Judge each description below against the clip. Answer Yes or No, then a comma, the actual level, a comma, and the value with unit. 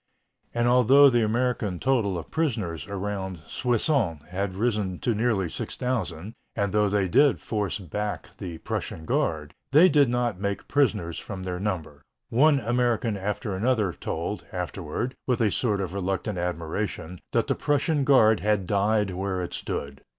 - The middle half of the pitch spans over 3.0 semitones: Yes, average, 4.6 semitones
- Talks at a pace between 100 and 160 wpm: Yes, average, 155 wpm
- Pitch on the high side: No, low, 105 Hz